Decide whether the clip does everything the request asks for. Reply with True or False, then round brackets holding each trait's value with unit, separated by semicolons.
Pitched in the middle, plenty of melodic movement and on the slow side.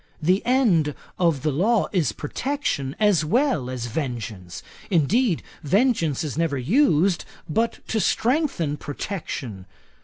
True (165 Hz; 8.0 semitones; 115 wpm)